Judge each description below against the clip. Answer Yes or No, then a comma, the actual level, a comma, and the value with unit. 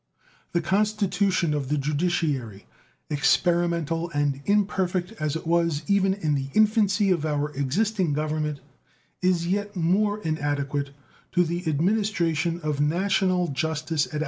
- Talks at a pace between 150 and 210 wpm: No, average, 140 wpm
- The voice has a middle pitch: Yes, medium, 170 Hz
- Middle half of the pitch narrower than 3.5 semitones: No, average, 4.2 semitones